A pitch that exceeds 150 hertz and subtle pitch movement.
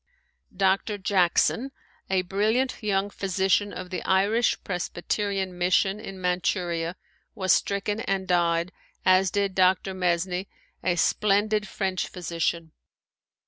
Yes: high, 190 Hz; narrow, 2.0 semitones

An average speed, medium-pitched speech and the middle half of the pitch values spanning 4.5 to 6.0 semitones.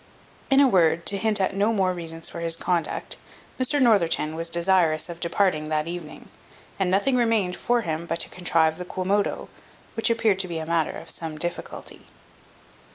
No: average, 180 wpm; medium, 180 Hz; average, 3.6 semitones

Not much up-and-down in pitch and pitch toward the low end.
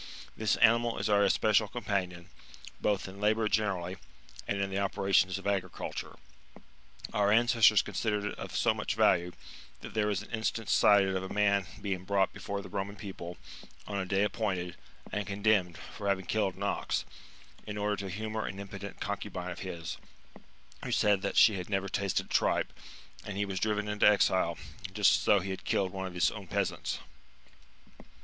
Yes: narrow, 1.7 semitones; low, 100 Hz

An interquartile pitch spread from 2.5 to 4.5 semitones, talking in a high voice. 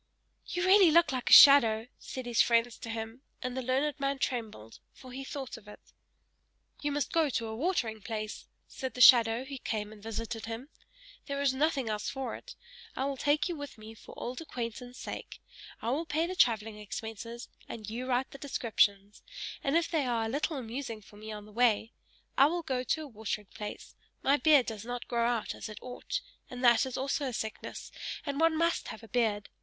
Yes: average, 4.0 semitones; high, 245 Hz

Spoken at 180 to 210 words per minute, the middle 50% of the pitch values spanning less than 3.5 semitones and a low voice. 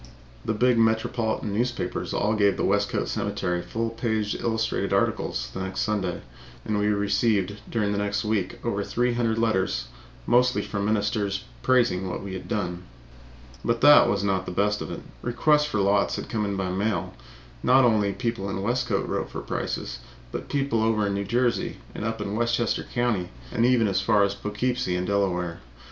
Yes: average, 190 wpm; average, 2.9 semitones; low, 105 Hz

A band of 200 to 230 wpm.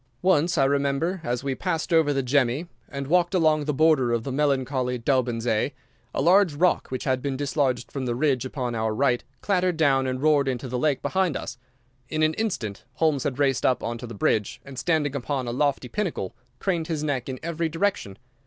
Yes: fast, 205 wpm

